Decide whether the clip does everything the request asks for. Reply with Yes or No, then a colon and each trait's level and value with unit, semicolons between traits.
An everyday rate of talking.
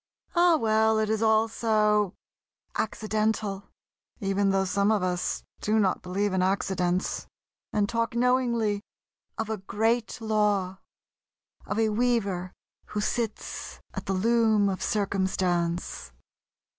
No: slow, 120 wpm